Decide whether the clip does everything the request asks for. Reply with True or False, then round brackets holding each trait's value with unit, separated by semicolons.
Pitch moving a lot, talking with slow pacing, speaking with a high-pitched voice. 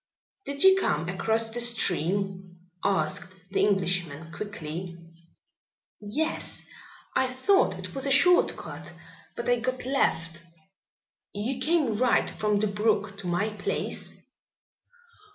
True (6.0 semitones; 120 wpm; 210 Hz)